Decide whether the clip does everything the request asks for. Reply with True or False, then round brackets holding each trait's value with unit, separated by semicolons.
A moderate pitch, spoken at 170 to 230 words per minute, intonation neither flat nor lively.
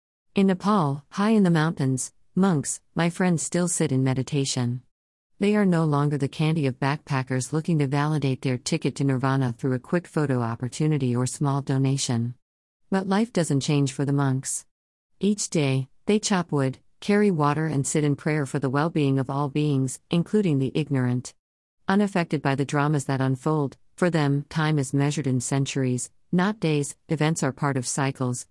True (145 Hz; 175 wpm; 3.4 semitones)